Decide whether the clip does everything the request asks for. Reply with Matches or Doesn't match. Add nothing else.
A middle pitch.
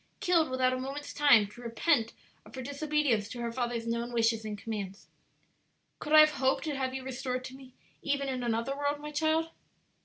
Doesn't match